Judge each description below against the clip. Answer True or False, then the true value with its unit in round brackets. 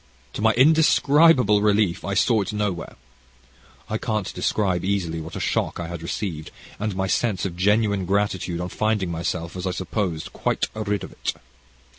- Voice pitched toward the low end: True (100 Hz)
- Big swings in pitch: False (3.4 semitones)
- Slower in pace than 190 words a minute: True (170 wpm)